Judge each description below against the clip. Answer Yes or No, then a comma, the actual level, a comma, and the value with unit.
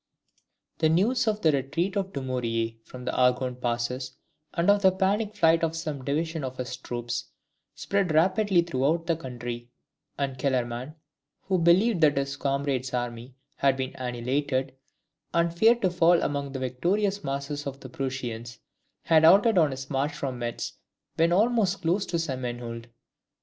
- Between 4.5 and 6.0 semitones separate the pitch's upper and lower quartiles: Yes, average, 5.2 semitones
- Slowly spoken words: No, average, 160 wpm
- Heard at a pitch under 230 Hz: Yes, medium, 140 Hz